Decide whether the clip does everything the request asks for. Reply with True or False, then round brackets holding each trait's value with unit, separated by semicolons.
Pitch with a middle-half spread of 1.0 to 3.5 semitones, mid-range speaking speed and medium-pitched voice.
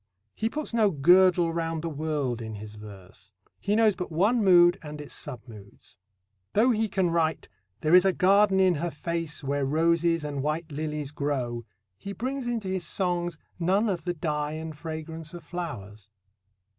False (4.1 semitones; 175 wpm; 165 Hz)